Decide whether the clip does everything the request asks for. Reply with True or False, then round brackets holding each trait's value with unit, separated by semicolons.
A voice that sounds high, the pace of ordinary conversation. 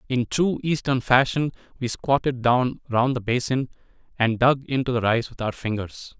False (125 Hz; 175 wpm)